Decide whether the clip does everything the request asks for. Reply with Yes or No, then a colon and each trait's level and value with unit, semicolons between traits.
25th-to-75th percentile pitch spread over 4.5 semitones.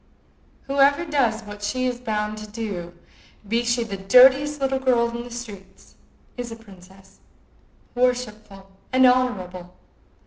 No: average, 3.8 semitones